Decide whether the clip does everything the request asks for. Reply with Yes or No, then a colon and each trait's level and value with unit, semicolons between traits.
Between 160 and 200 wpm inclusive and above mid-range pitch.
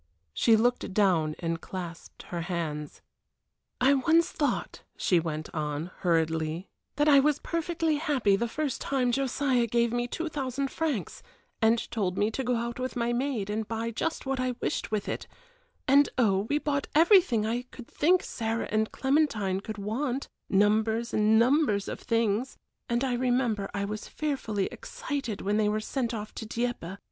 Yes: average, 170 wpm; high, 230 Hz